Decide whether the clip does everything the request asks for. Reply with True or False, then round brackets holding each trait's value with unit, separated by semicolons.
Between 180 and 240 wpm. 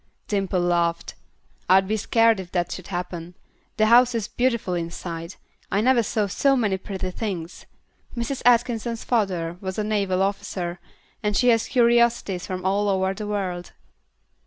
False (155 wpm)